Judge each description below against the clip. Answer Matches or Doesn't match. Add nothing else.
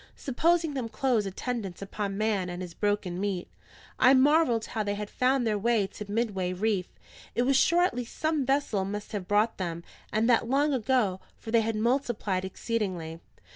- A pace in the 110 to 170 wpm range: Doesn't match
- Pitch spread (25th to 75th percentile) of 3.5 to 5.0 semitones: Matches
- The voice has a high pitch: Matches